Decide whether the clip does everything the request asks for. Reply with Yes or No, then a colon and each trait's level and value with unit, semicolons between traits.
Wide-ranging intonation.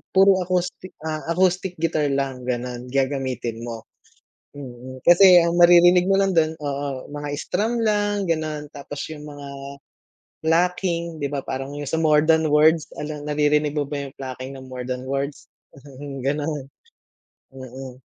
No: average, 3.9 semitones